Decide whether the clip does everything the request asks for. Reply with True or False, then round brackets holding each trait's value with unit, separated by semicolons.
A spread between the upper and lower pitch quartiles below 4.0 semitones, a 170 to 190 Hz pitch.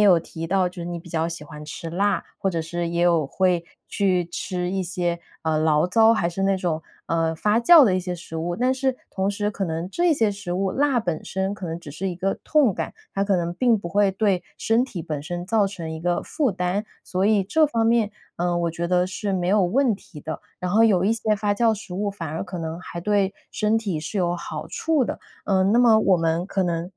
True (3.4 semitones; 185 Hz)